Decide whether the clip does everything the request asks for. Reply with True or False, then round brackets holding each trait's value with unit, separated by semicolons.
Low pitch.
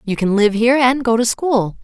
False (230 Hz)